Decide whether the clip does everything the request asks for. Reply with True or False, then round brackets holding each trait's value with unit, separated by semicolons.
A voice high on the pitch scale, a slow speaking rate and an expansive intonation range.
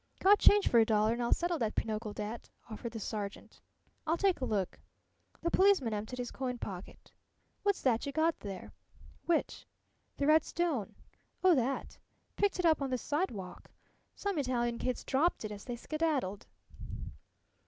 False (255 Hz; 165 wpm; 7.0 semitones)